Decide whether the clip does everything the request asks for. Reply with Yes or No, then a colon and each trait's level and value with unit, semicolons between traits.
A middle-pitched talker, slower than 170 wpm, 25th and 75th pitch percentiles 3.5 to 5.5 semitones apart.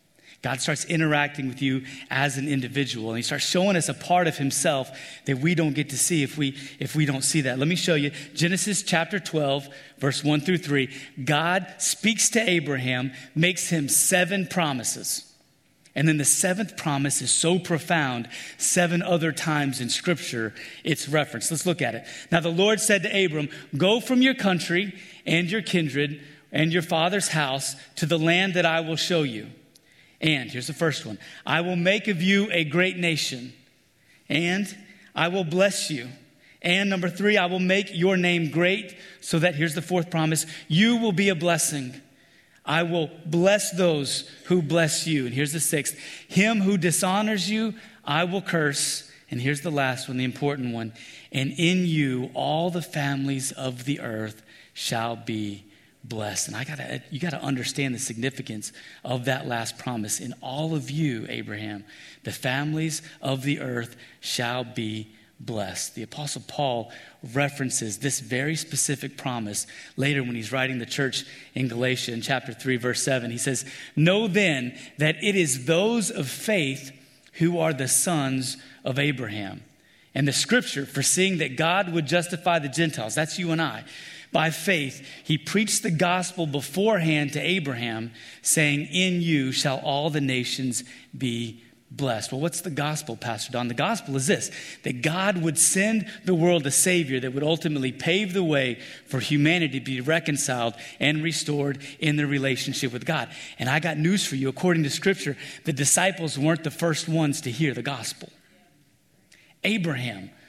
No: medium, 150 Hz; average, 175 wpm; average, 4.5 semitones